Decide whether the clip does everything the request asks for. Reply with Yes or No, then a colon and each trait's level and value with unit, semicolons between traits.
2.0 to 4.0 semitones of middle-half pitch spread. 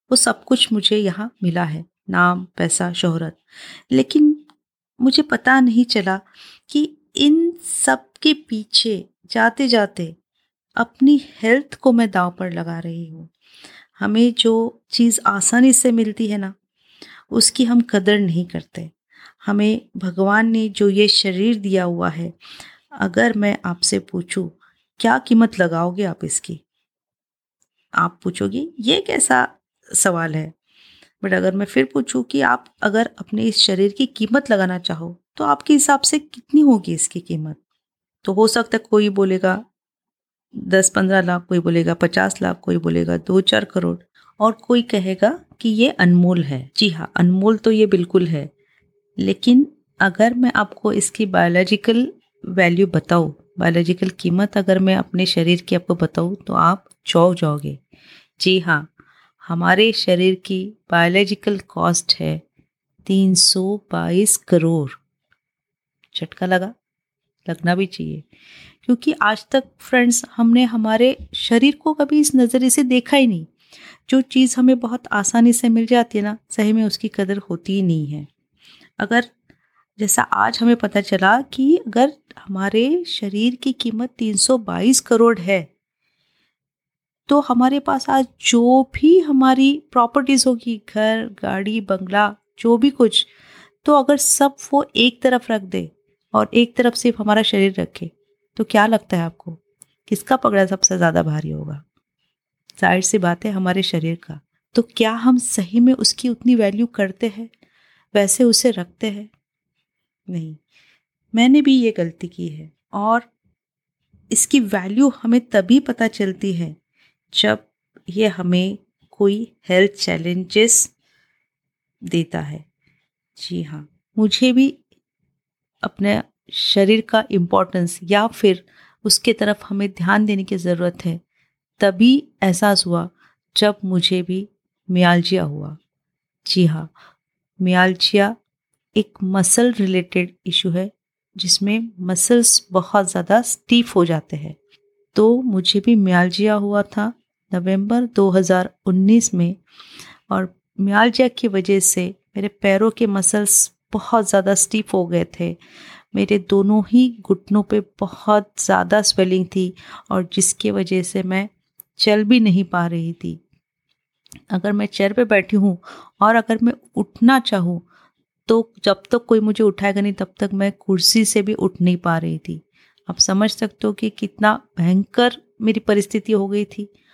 No: average, 4.4 semitones